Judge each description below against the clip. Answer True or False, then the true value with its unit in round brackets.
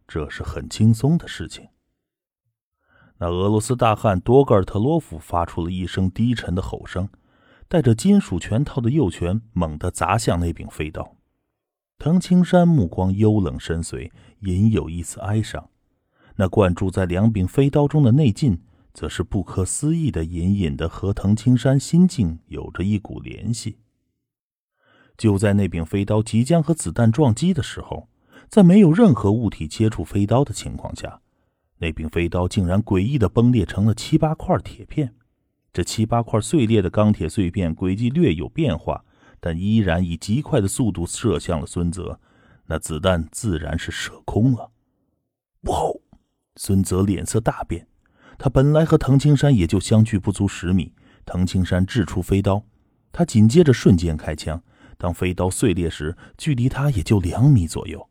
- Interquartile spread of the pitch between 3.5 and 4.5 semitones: False (5.5 semitones)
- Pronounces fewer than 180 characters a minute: False (245 characters per minute)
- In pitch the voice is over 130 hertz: False (105 Hz)